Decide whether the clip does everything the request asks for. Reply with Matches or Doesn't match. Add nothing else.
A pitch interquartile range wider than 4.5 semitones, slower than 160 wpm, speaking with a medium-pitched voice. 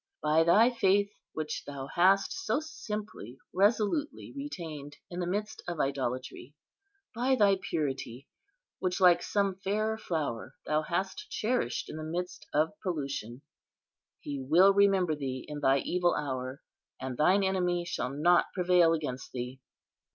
Matches